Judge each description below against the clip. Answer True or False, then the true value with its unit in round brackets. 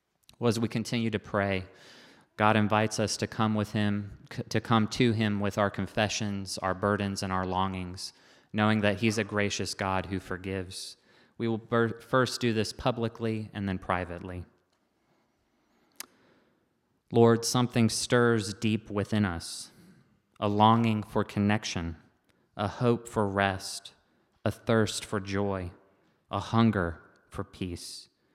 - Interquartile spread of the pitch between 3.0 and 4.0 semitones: False (2.6 semitones)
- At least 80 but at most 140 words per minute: True (135 wpm)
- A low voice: True (105 Hz)